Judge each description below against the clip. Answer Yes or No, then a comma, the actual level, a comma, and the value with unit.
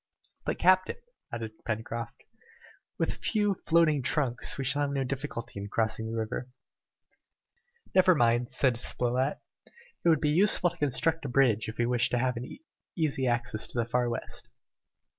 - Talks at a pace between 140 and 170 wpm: Yes, average, 165 wpm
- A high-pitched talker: No, low, 125 Hz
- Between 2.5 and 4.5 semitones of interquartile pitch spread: Yes, average, 4.1 semitones